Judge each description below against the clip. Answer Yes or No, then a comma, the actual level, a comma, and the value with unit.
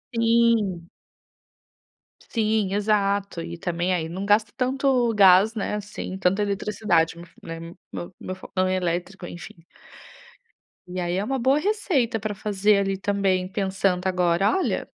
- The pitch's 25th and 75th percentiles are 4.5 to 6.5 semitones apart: No, average, 3.0 semitones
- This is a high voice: Yes, high, 195 Hz